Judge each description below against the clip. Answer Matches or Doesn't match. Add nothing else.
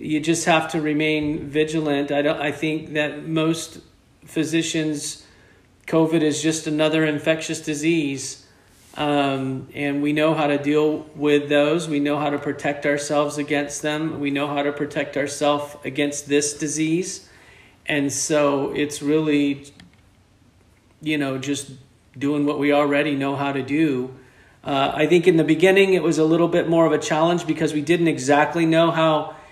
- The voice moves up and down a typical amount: Doesn't match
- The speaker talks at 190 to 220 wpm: Doesn't match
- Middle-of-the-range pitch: Matches